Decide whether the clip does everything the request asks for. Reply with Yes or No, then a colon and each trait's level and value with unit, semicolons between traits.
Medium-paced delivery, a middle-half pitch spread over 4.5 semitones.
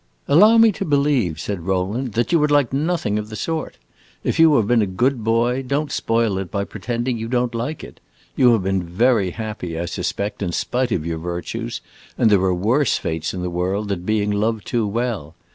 No: fast, 210 wpm; average, 5.0 semitones